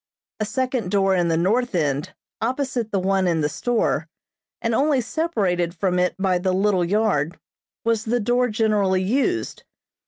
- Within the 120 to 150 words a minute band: No, average, 160 wpm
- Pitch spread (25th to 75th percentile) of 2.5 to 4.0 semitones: No, average, 5.0 semitones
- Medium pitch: No, high, 205 Hz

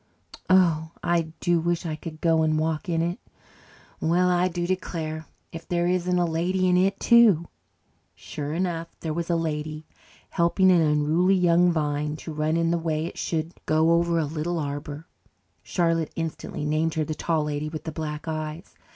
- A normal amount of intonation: No, narrow, 1.9 semitones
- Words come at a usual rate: Yes, average, 180 wpm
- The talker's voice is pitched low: No, medium, 165 Hz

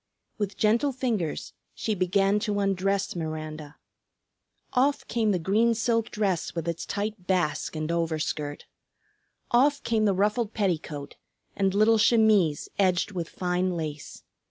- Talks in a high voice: Yes, high, 195 Hz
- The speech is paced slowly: Yes, slow, 130 wpm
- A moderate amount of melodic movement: Yes, average, 4.5 semitones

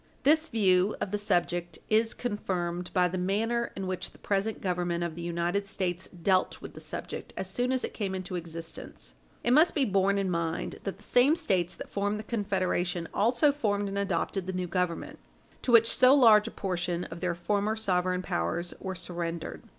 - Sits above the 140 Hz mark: Yes, high, 190 Hz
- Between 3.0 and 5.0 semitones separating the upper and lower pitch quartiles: Yes, average, 3.3 semitones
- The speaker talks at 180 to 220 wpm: Yes, average, 195 wpm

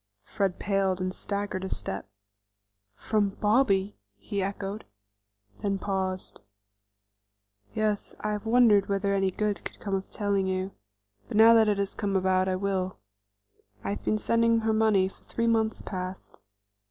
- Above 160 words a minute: No, average, 155 wpm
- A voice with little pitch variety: Yes, narrow, 2.0 semitones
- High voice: Yes, high, 200 Hz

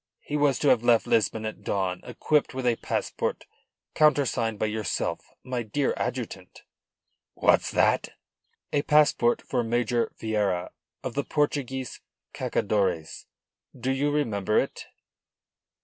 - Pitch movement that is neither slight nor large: Yes, average, 4.4 semitones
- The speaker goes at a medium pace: No, slow, 125 wpm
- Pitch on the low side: Yes, low, 120 Hz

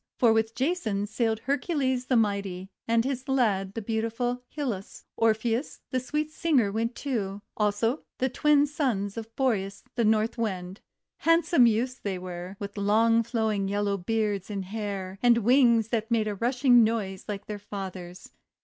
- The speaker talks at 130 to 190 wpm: Yes, average, 160 wpm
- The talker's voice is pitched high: Yes, high, 225 Hz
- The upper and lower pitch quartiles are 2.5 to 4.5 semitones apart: Yes, average, 3.7 semitones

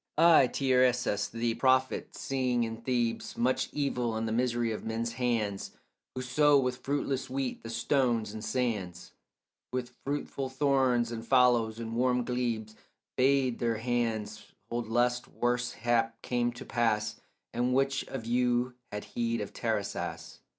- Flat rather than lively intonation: Yes, narrow, 2.1 semitones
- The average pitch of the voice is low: Yes, low, 120 Hz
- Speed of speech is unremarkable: Yes, average, 145 wpm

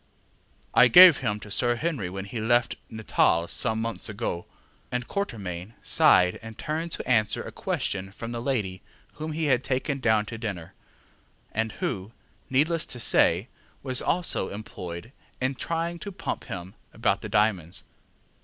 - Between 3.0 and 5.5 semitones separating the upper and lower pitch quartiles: Yes, average, 5.1 semitones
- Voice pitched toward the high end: No, low, 115 Hz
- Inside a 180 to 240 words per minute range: No, average, 160 wpm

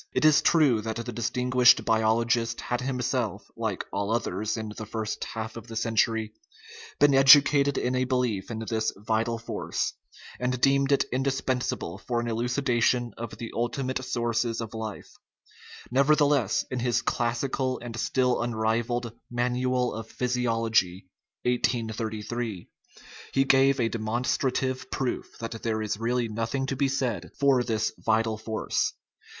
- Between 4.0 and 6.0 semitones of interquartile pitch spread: No, narrow, 2.4 semitones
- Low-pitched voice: Yes, low, 120 Hz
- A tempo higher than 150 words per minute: No, average, 145 wpm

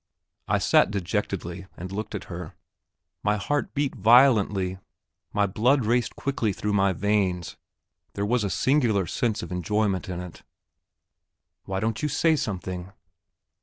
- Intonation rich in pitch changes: No, average, 4.1 semitones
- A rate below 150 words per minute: Yes, average, 140 wpm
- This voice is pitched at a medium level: No, low, 105 Hz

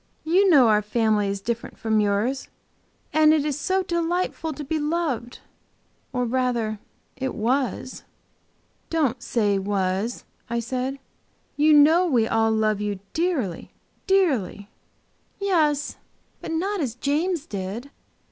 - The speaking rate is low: Yes, slow, 130 wpm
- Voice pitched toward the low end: No, very high, 260 Hz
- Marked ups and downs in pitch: Yes, wide, 6.3 semitones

